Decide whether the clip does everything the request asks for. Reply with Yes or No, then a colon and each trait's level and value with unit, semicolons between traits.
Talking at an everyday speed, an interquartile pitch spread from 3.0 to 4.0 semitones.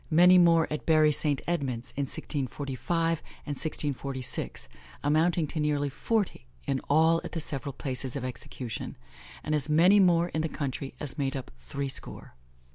Yes: average, 155 wpm; average, 3.4 semitones